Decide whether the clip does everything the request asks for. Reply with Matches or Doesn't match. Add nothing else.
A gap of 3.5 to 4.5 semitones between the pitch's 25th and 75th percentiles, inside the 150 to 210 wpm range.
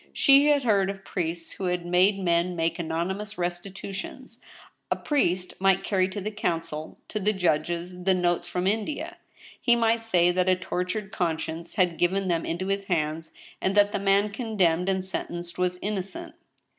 Doesn't match